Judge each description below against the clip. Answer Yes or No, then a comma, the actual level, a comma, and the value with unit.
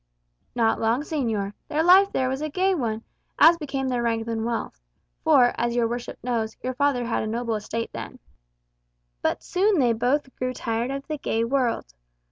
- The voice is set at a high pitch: Yes, high, 245 Hz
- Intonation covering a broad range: No, average, 3.7 semitones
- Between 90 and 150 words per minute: No, average, 185 wpm